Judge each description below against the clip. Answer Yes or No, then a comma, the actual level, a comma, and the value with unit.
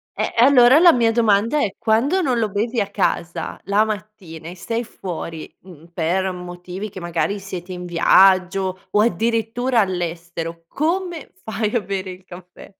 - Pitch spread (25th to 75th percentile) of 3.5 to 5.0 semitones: Yes, average, 4.4 semitones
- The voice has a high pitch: Yes, high, 195 Hz